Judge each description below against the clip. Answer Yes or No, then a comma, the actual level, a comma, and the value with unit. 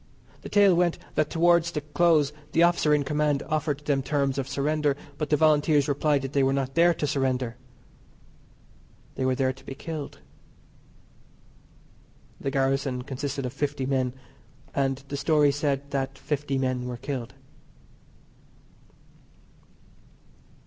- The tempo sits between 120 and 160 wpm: Yes, average, 140 wpm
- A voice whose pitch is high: No, medium, 140 Hz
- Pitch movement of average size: No, narrow, 2.0 semitones